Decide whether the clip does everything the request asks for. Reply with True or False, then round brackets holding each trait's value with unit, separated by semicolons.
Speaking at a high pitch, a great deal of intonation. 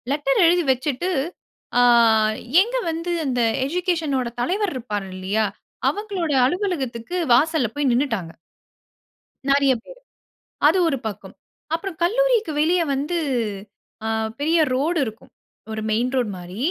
True (290 Hz; 6.3 semitones)